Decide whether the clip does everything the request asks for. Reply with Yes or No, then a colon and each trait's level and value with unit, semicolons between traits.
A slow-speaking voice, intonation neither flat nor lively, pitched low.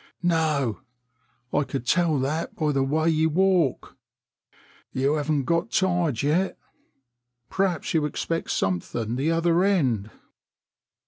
No: slow, 120 wpm; average, 3.9 semitones; medium, 155 Hz